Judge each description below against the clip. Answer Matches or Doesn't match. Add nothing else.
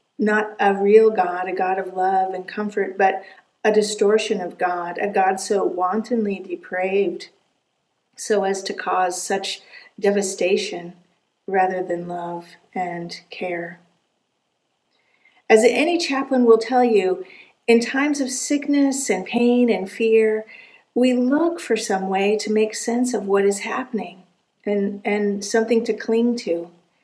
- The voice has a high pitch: Matches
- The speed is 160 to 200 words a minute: Doesn't match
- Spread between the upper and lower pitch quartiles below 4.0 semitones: Matches